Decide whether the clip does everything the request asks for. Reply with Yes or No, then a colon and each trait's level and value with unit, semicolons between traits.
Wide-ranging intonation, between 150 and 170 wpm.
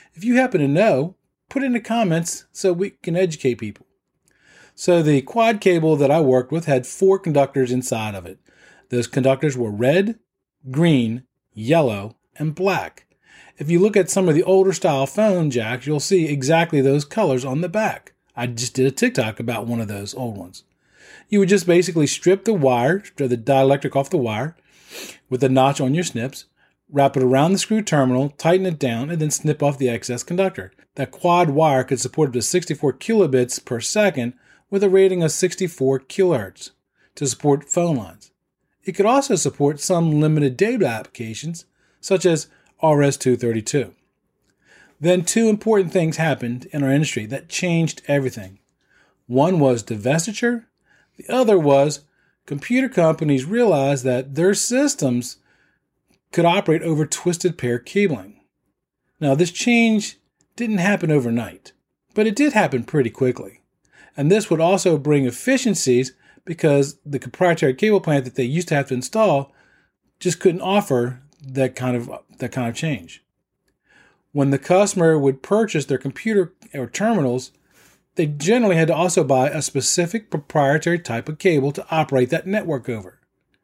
Yes: wide, 6.0 semitones; average, 165 wpm